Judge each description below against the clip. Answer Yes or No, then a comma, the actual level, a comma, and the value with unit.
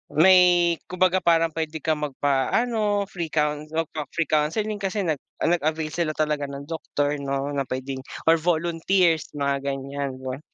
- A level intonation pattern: No, average, 3.4 semitones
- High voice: No, medium, 155 Hz